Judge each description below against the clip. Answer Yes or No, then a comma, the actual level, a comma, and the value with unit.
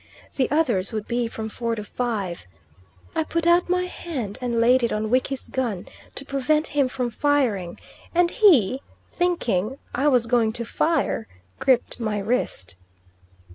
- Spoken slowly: No, average, 155 wpm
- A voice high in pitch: Yes, high, 245 Hz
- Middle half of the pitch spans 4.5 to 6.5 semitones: Yes, average, 4.9 semitones